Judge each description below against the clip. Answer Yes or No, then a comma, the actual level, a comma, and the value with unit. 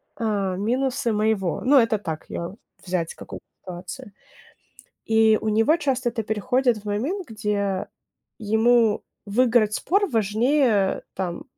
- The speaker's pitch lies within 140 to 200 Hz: No, high, 220 Hz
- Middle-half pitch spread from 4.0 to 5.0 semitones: No, average, 3.3 semitones